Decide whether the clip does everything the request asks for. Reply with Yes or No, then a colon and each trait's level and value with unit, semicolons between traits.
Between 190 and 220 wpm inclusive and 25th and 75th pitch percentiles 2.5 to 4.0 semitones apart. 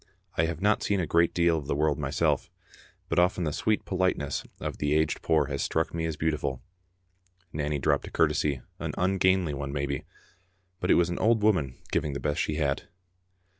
Yes: average, 195 wpm; average, 3.5 semitones